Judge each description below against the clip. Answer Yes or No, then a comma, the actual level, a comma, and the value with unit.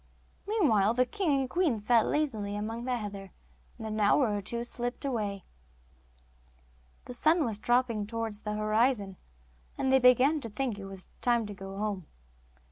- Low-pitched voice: No, high, 230 Hz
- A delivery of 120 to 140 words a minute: No, average, 165 wpm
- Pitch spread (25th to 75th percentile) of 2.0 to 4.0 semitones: Yes, average, 3.5 semitones